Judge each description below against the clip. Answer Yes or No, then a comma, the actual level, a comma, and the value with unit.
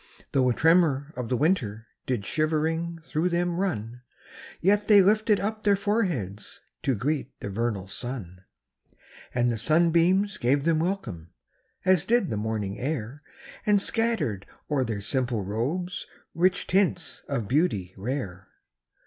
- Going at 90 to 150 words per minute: Yes, average, 140 wpm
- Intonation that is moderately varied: No, wide, 8.2 semitones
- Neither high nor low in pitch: Yes, medium, 145 Hz